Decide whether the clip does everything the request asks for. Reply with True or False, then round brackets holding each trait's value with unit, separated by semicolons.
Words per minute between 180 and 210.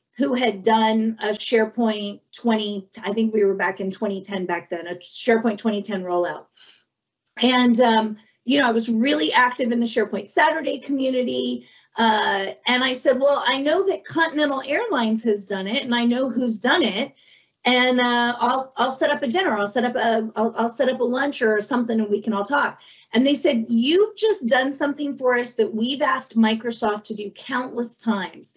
True (195 wpm)